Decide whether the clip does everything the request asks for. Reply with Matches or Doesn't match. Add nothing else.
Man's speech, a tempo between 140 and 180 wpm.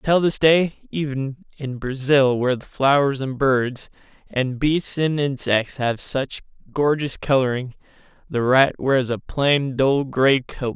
Matches